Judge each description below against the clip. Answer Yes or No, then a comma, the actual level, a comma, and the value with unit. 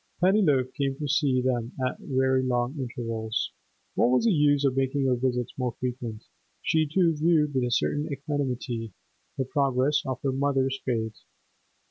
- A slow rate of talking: No, average, 160 wpm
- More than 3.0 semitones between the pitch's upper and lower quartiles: No, narrow, 2.6 semitones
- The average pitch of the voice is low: Yes, low, 130 Hz